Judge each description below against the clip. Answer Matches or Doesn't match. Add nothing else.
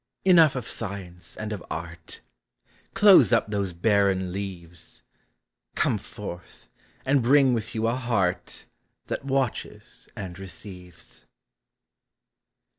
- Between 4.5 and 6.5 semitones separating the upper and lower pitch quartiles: Matches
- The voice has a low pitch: Matches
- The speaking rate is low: Matches